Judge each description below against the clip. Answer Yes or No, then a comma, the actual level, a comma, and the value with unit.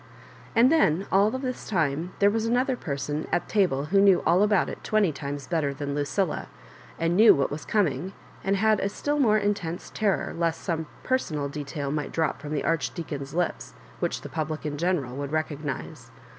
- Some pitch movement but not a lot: No, wide, 5.7 semitones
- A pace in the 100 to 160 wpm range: No, average, 185 wpm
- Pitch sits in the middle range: Yes, medium, 165 Hz